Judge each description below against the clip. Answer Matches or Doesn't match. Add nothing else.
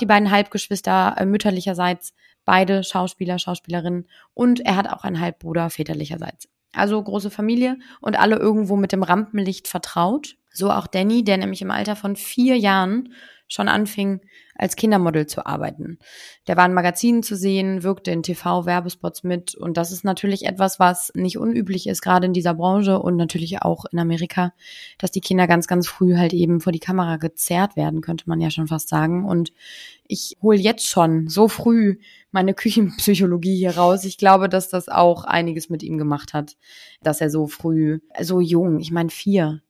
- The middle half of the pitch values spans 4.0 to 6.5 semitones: Doesn't match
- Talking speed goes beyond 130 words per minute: Matches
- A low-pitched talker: Doesn't match